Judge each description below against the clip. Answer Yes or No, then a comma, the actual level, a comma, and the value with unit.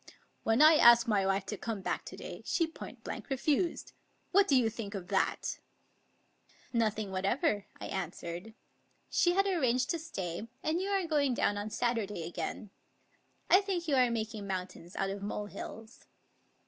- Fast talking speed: No, average, 180 wpm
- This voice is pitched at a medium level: No, high, 225 Hz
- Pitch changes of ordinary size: No, wide, 7.4 semitones